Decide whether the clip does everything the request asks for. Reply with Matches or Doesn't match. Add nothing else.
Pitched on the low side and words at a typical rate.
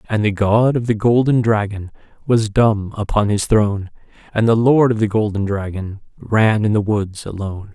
Matches